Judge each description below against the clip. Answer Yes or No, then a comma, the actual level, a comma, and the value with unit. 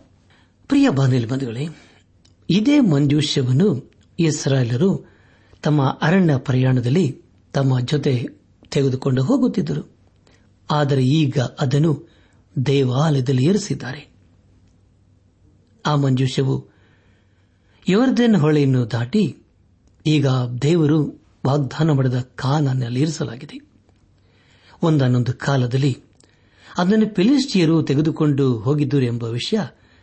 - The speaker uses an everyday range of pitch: Yes, average, 4.8 semitones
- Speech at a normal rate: Yes, average, 75 wpm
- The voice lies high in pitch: No, low, 135 Hz